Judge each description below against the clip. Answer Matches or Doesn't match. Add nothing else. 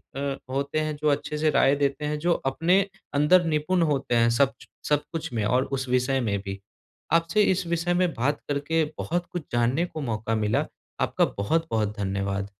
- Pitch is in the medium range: Matches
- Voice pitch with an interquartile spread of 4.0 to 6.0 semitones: Matches